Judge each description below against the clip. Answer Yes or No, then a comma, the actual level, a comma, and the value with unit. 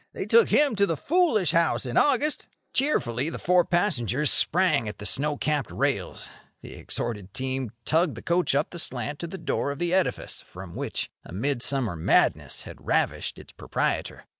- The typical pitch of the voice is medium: Yes, medium, 150 Hz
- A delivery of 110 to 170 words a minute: No, average, 185 wpm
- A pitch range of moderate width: No, wide, 6.9 semitones